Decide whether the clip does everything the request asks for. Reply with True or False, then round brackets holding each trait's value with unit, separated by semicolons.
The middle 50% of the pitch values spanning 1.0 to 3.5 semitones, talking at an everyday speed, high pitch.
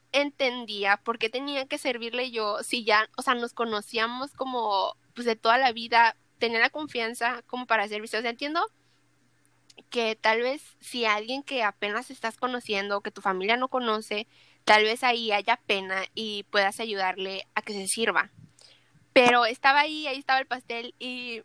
True (2.9 semitones; 175 wpm; 230 Hz)